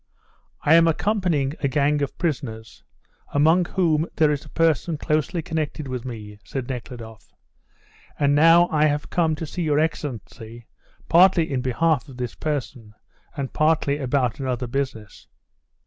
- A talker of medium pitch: Yes, medium, 145 Hz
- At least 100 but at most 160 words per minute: Yes, average, 150 wpm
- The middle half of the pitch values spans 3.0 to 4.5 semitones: Yes, average, 4.2 semitones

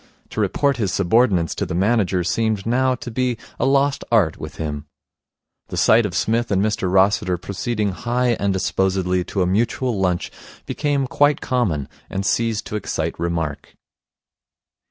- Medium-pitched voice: No, low, 105 Hz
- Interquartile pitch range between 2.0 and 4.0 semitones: No, average, 4.7 semitones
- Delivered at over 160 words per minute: No, average, 155 wpm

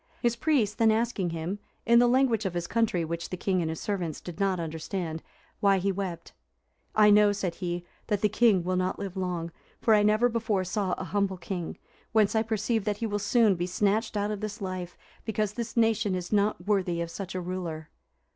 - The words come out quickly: Yes, fast, 210 wpm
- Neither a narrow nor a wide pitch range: Yes, average, 3.2 semitones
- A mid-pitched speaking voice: No, high, 200 Hz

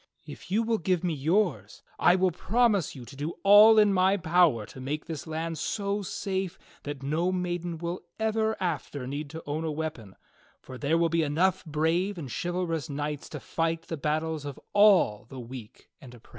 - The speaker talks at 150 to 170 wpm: No, average, 200 wpm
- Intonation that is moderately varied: Yes, average, 4.2 semitones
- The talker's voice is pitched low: No, medium, 165 Hz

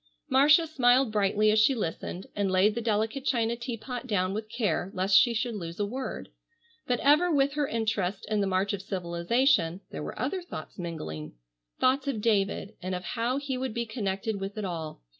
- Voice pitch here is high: Yes, high, 215 Hz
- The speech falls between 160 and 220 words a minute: Yes, average, 195 wpm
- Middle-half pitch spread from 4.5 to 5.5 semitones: Yes, average, 4.8 semitones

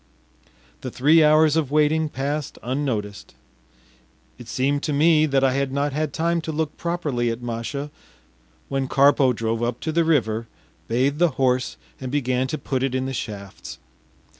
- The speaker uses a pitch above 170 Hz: No, medium, 140 Hz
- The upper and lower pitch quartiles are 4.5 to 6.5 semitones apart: No, average, 3.5 semitones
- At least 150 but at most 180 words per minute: Yes, average, 165 wpm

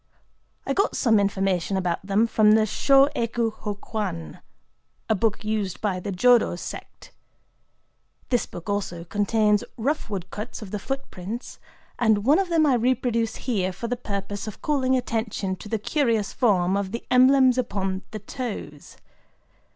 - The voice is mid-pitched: No, high, 215 Hz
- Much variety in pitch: No, average, 3.9 semitones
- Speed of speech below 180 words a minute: Yes, average, 150 wpm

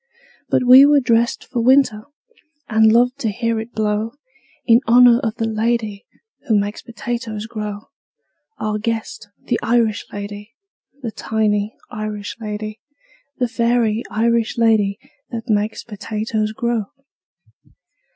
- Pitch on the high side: Yes, high, 225 Hz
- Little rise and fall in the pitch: Yes, narrow, 1.8 semitones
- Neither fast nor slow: No, slow, 125 wpm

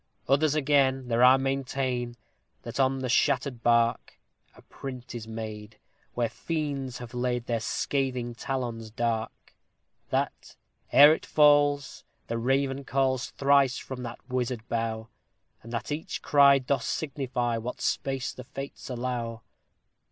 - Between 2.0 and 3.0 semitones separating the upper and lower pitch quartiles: Yes, narrow, 2.6 semitones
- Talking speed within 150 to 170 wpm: No, slow, 135 wpm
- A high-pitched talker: No, low, 125 Hz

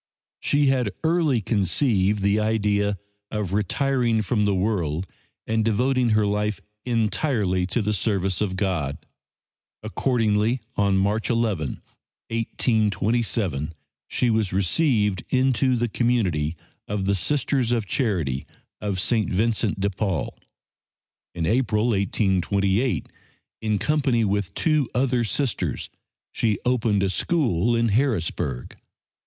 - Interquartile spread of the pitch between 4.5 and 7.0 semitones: No, average, 3.7 semitones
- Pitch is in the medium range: No, low, 105 Hz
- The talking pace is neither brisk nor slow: No, slow, 115 wpm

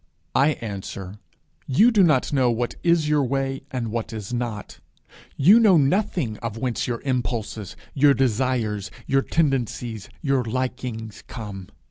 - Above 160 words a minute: No, average, 140 wpm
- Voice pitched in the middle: No, low, 125 Hz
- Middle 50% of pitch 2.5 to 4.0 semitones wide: Yes, average, 3.7 semitones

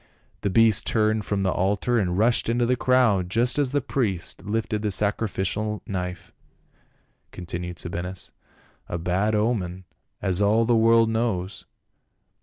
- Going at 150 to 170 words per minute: No, average, 140 wpm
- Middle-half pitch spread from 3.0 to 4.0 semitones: Yes, average, 3.7 semitones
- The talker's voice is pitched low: Yes, low, 105 Hz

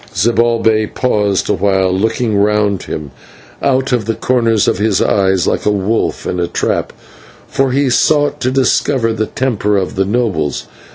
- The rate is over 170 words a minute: No, average, 160 wpm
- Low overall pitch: Yes, low, 110 Hz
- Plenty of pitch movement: No, average, 3.8 semitones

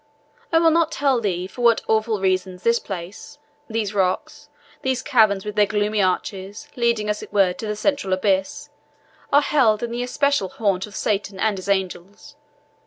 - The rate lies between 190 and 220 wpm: No, average, 175 wpm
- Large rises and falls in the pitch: No, average, 3.7 semitones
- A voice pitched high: Yes, high, 210 Hz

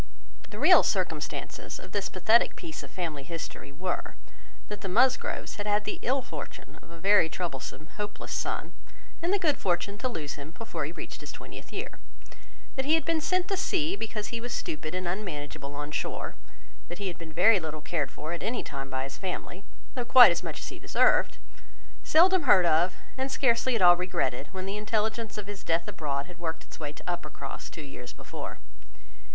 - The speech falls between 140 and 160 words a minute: No, average, 200 wpm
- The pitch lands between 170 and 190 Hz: Yes, medium, 185 Hz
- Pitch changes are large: Yes, wide, 6.4 semitones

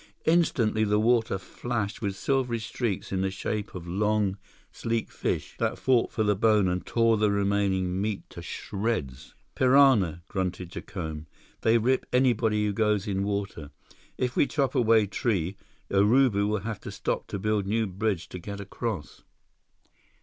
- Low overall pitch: Yes, low, 105 Hz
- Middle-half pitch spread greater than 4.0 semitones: No, average, 3.0 semitones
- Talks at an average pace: Yes, average, 155 wpm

